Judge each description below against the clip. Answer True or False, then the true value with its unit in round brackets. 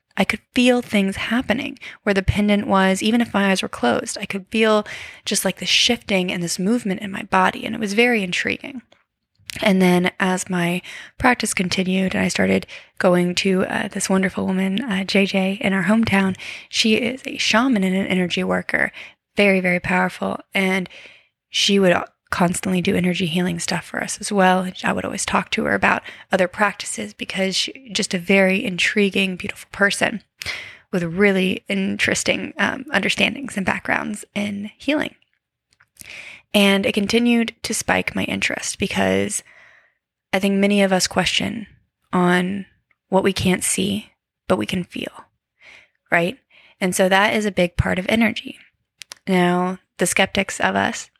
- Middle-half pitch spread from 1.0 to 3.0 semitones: True (2.4 semitones)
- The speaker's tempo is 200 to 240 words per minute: False (165 wpm)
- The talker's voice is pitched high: True (195 Hz)